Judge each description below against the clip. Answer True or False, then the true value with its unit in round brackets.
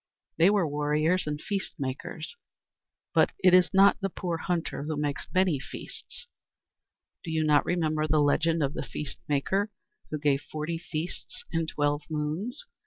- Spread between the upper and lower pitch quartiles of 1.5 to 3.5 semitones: True (3.1 semitones)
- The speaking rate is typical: True (160 wpm)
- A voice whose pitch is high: False (155 Hz)